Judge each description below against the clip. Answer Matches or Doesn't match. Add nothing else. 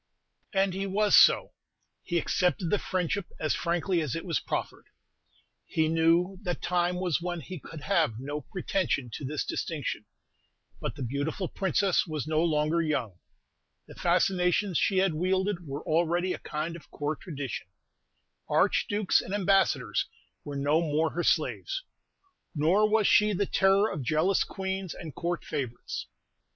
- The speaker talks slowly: Doesn't match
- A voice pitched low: Doesn't match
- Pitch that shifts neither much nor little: Matches